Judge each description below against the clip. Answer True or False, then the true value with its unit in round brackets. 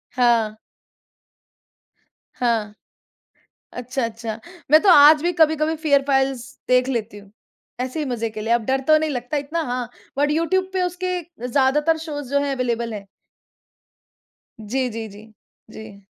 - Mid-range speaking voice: False (260 Hz)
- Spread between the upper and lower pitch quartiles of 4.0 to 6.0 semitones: True (5.0 semitones)